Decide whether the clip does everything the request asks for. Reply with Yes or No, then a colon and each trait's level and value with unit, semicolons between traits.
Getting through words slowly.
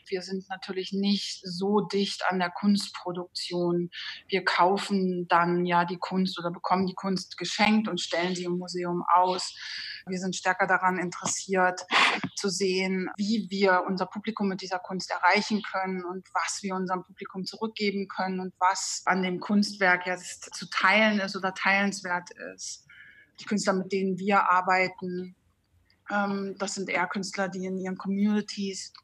No: average, 155 wpm